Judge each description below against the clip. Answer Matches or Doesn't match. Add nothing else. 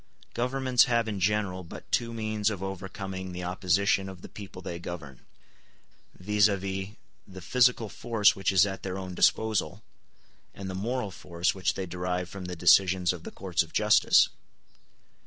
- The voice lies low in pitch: Matches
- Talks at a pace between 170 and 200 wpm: Doesn't match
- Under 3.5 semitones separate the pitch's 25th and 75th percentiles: Matches